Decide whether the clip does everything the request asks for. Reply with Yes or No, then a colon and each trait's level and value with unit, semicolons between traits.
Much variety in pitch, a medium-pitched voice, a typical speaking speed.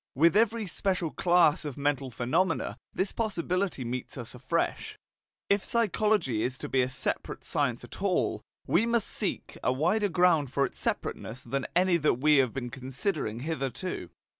Yes: wide, 6.3 semitones; medium, 155 Hz; average, 165 wpm